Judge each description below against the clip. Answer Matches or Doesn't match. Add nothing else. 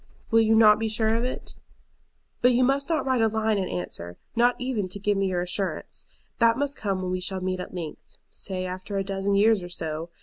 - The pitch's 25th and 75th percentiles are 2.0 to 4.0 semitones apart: Matches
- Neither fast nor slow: Doesn't match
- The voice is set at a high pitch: Matches